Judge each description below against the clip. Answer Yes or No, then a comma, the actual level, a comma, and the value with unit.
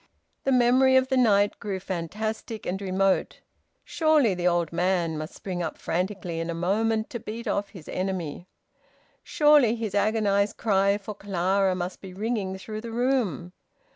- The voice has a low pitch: No, high, 200 Hz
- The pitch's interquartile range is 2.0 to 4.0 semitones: Yes, average, 3.6 semitones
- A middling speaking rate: Yes, average, 160 wpm